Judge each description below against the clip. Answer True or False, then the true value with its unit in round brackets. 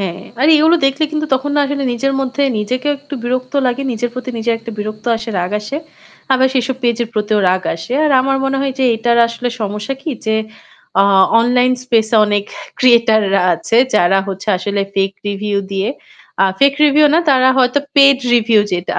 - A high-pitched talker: True (240 Hz)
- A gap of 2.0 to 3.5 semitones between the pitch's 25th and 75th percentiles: False (4.3 semitones)